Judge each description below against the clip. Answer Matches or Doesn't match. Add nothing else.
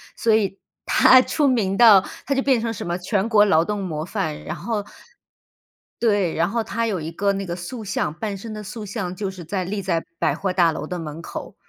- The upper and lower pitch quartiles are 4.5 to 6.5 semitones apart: Doesn't match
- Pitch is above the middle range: Matches